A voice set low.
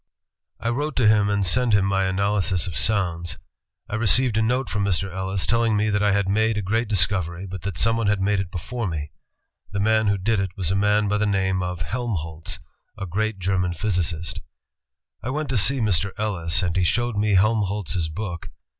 Yes: low, 100 Hz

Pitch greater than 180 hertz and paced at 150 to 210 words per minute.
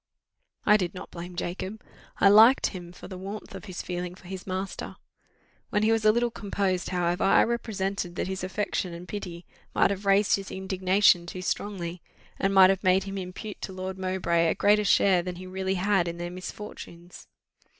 Yes: high, 190 Hz; average, 190 wpm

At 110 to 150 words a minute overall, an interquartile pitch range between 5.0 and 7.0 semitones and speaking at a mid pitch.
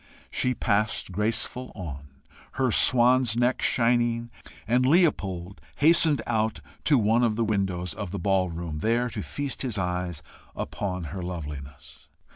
No: average, 140 wpm; wide, 5.4 semitones; low, 105 Hz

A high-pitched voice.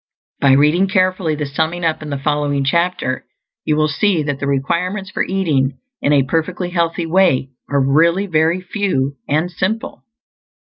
No: medium, 160 Hz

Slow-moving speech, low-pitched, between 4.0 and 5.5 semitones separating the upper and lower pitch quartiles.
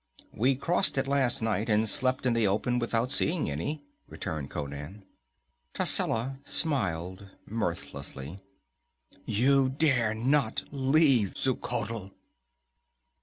Yes: slow, 105 wpm; low, 115 Hz; average, 5.2 semitones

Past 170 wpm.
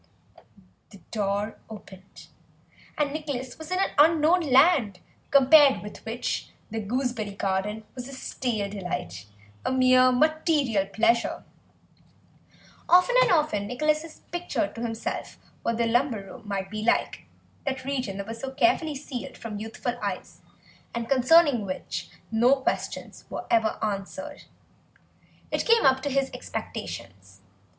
No: slow, 135 wpm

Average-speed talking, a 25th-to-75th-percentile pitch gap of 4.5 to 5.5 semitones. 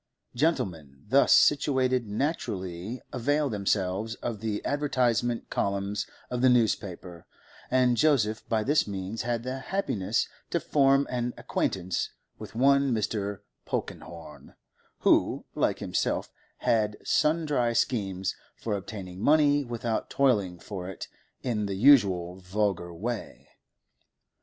No: slow, 115 wpm; average, 5.1 semitones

